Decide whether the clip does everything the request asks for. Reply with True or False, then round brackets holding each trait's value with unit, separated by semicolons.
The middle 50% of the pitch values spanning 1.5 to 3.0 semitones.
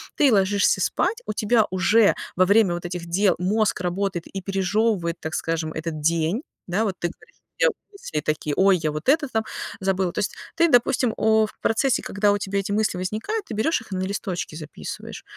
False (4.0 semitones)